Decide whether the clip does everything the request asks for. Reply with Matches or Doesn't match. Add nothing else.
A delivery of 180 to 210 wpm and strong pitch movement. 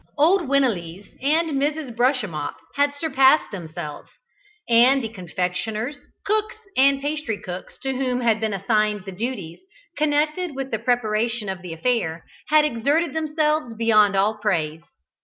Doesn't match